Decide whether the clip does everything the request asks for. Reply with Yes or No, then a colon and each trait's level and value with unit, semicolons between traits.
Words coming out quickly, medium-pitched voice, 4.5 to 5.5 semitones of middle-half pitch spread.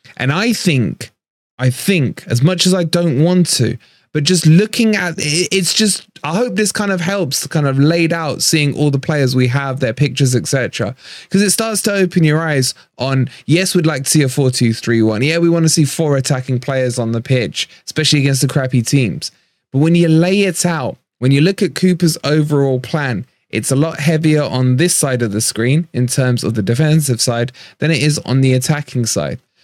Yes: fast, 215 wpm; medium, 145 Hz; average, 4.9 semitones